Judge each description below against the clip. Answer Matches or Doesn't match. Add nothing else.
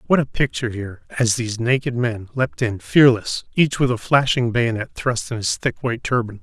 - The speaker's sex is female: Doesn't match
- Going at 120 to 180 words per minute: Doesn't match